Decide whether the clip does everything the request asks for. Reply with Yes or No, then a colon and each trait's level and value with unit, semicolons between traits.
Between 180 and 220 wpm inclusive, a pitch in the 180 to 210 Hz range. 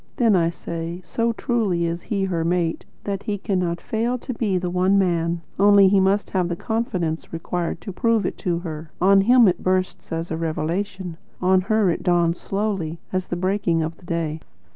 Yes: average, 195 wpm; medium, 185 Hz